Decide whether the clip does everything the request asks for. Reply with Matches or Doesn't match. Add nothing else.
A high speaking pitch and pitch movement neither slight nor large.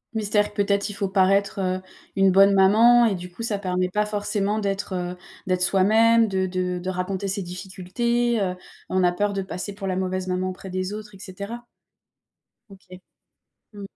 Doesn't match